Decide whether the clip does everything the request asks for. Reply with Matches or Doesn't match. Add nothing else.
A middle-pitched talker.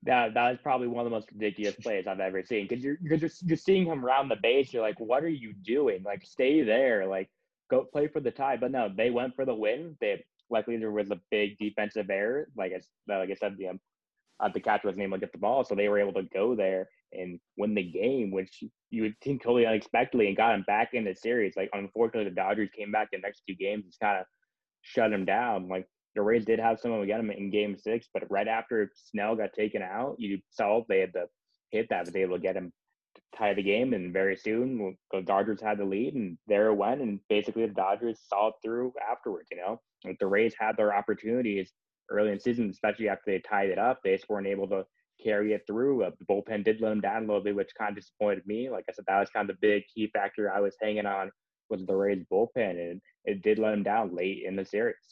Doesn't match